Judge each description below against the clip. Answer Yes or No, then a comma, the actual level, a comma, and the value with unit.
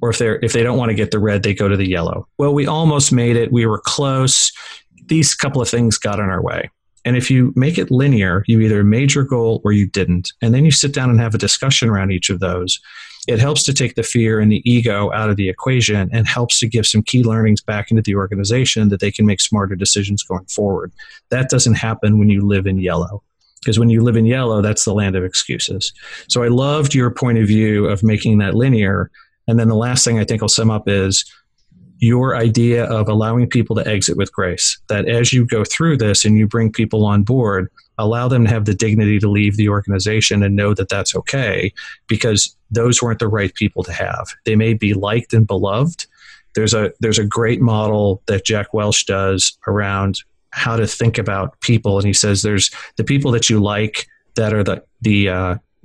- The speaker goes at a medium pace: No, fast, 230 wpm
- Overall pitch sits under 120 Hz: Yes, low, 110 Hz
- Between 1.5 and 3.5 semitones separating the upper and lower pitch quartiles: Yes, average, 2.7 semitones